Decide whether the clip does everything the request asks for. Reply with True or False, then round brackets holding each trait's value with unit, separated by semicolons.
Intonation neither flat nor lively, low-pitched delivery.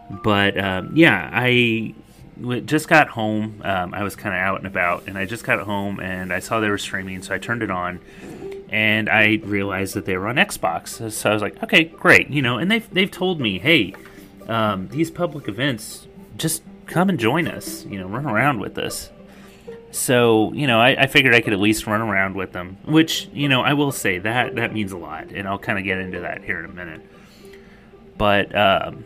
False (6.8 semitones; 110 Hz)